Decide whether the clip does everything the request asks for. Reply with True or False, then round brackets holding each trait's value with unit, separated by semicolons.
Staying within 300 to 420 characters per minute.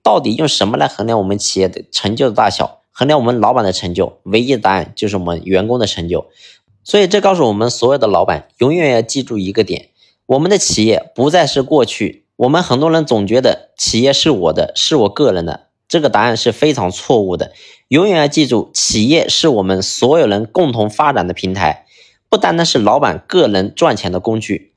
True (320 characters per minute)